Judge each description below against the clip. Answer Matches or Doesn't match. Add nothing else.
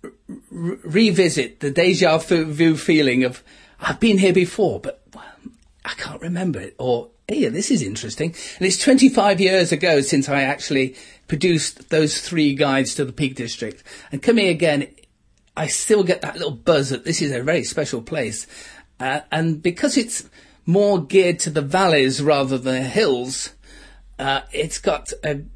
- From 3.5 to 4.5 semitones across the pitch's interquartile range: Doesn't match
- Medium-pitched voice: Matches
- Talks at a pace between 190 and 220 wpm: Doesn't match